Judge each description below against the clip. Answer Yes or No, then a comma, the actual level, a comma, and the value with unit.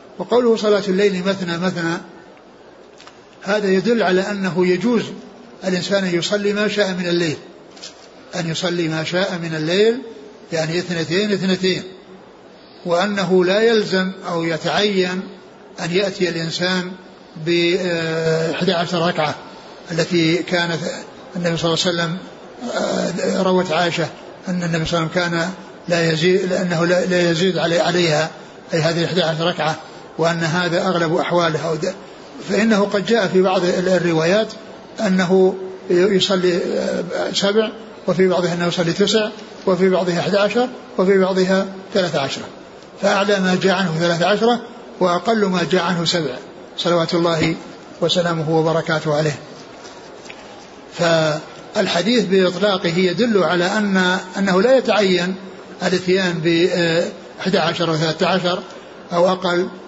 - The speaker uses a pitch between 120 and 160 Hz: No, medium, 180 Hz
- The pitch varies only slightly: Yes, narrow, 2.2 semitones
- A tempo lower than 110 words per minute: No, average, 120 wpm